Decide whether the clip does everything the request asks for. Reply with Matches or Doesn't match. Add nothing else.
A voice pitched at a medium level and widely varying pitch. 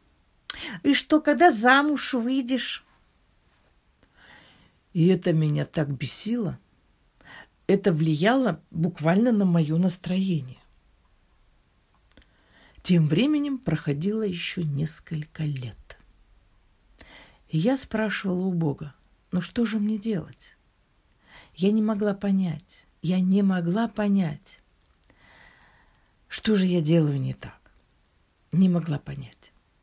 Matches